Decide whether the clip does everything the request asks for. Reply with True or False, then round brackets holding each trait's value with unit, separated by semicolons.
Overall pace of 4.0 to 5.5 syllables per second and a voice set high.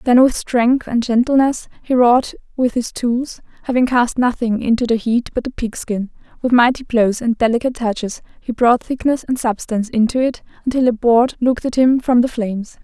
True (5.3 syllables/s; 240 Hz)